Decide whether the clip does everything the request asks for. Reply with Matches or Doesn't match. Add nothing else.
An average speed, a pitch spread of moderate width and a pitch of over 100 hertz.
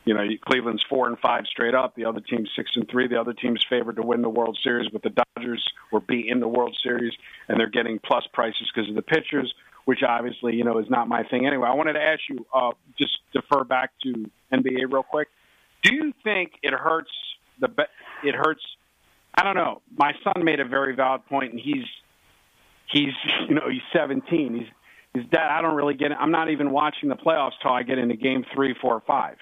Doesn't match